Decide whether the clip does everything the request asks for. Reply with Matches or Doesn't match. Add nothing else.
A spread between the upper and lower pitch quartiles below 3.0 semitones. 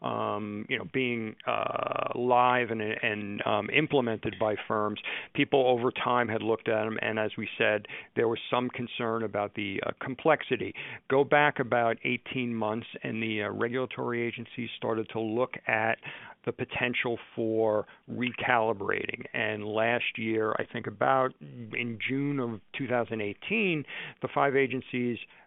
Matches